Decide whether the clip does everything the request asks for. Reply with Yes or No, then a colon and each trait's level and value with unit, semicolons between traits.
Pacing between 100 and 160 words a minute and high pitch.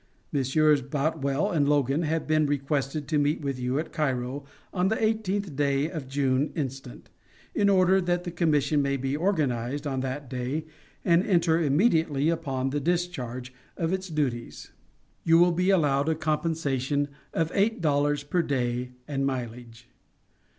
No: average, 155 wpm; medium, 145 Hz